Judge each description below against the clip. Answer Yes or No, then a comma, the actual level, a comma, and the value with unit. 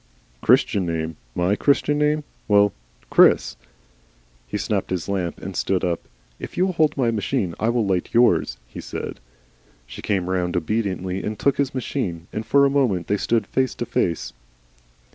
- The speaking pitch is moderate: No, low, 100 Hz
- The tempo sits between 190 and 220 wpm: No, average, 170 wpm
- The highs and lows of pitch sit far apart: Yes, wide, 6.6 semitones